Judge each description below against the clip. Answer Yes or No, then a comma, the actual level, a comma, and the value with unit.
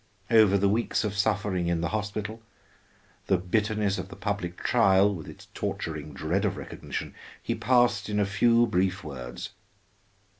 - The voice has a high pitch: No, low, 100 Hz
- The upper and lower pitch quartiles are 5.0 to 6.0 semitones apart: No, average, 2.8 semitones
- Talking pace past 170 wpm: No, average, 155 wpm